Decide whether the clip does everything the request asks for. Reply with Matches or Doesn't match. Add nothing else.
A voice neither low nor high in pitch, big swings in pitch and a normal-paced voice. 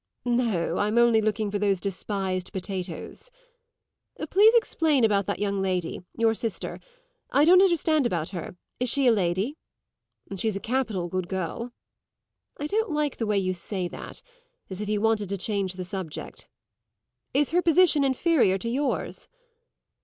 Doesn't match